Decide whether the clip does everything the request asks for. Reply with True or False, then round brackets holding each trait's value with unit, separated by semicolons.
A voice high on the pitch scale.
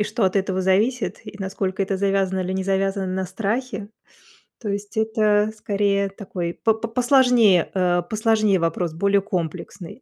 True (200 Hz)